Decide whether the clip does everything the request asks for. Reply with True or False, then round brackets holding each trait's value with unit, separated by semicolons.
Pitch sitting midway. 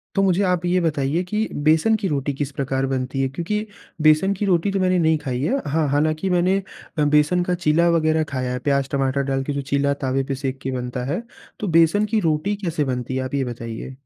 True (150 Hz)